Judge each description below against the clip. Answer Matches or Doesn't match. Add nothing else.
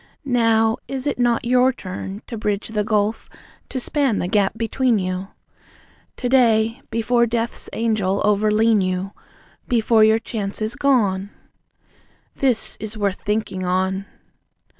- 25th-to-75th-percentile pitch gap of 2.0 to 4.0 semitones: Matches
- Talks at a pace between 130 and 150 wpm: Matches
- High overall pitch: Matches